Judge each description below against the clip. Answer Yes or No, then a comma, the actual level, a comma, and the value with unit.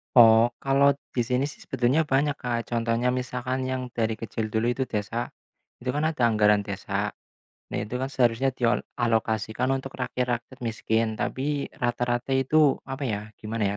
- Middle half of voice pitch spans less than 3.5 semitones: Yes, narrow, 2.6 semitones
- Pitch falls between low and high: No, low, 120 Hz